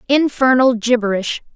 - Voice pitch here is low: No, high, 245 Hz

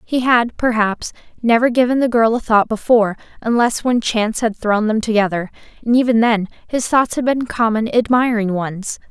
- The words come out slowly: No, average, 180 wpm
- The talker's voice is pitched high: Yes, high, 230 Hz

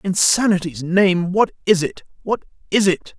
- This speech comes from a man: No, female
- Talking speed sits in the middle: Yes, average, 150 wpm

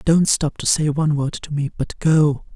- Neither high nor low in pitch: Yes, medium, 150 Hz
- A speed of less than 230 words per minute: No, fast, 235 wpm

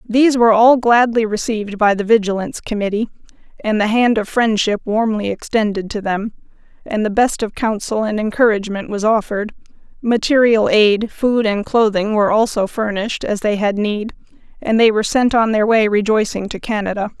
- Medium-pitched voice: No, high, 215 Hz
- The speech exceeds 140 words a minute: Yes, average, 170 wpm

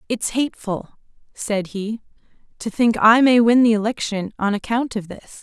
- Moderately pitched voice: No, high, 220 Hz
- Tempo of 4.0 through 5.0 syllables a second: Yes, 4.7 syllables/s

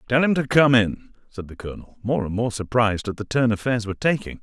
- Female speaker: No, male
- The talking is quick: Yes, fast, 245 wpm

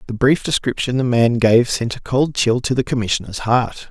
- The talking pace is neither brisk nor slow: No, fast, 215 wpm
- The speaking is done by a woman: No, male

